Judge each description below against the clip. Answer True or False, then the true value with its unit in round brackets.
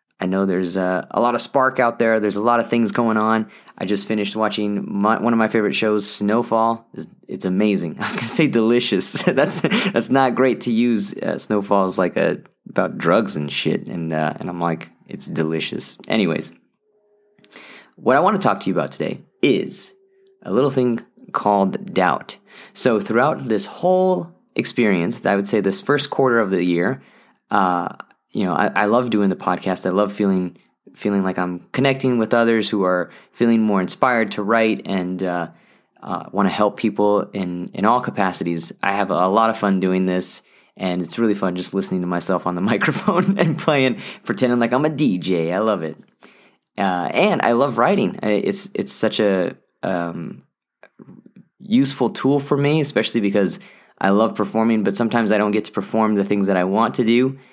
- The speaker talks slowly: False (195 wpm)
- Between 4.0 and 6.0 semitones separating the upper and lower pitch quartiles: True (4.4 semitones)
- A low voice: True (105 Hz)